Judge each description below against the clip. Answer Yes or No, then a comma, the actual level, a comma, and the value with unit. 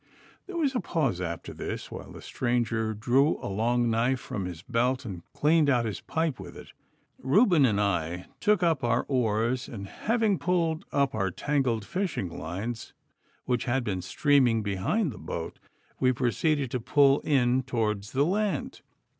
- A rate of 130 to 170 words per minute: Yes, average, 165 wpm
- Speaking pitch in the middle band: No, low, 125 Hz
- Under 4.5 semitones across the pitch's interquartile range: No, wide, 5.4 semitones